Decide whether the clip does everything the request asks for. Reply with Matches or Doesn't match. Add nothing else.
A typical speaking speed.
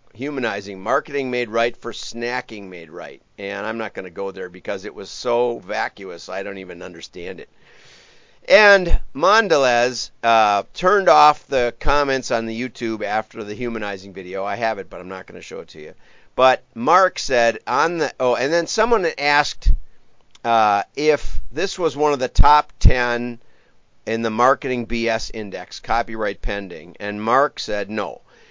Matches